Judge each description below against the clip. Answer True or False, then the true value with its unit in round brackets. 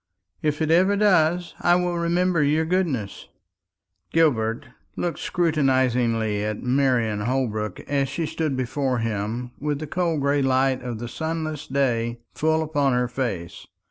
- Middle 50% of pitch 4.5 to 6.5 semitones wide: True (5.0 semitones)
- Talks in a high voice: False (135 Hz)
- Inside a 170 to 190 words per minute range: False (140 wpm)